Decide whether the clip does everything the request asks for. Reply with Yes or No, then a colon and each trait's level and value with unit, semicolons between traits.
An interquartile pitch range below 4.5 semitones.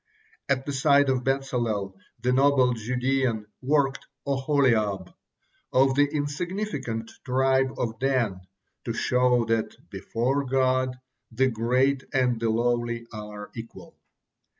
Yes: average, 2.8 semitones